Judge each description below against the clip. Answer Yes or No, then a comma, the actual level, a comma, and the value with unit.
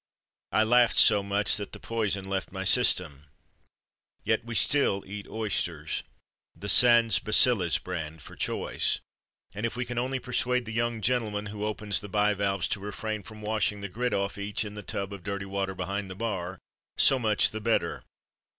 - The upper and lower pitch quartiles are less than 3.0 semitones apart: Yes, narrow, 2.5 semitones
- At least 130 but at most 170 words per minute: No, average, 180 wpm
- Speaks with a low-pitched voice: Yes, low, 105 Hz